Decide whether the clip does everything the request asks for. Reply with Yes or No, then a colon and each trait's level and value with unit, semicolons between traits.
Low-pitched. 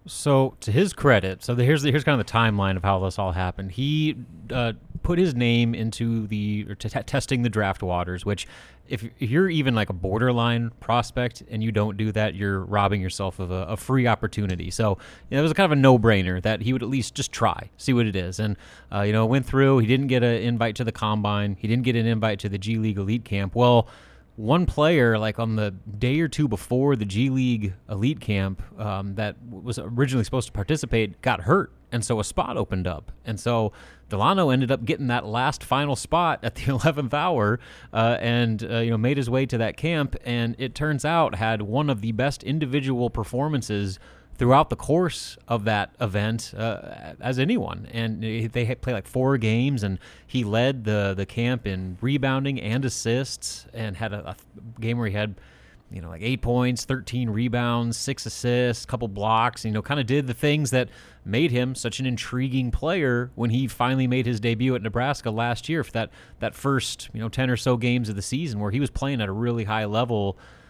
Yes: low, 115 Hz